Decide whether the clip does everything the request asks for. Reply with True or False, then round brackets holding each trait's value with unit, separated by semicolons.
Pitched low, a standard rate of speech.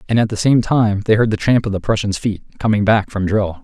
False (105 Hz; 280 wpm)